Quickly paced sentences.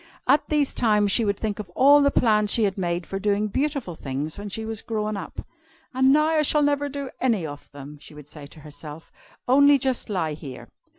Yes: fast, 220 wpm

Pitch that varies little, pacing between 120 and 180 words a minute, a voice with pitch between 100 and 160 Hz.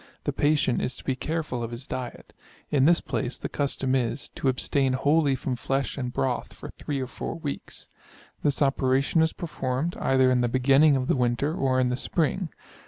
No: narrow, 2.3 semitones; average, 195 wpm; low, 135 Hz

